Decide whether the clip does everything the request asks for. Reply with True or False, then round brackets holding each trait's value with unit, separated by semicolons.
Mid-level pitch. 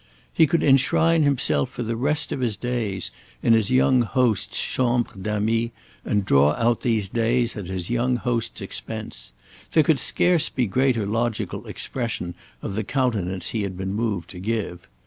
False (115 Hz)